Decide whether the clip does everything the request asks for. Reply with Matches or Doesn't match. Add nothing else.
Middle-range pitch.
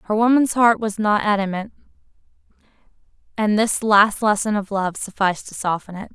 Doesn't match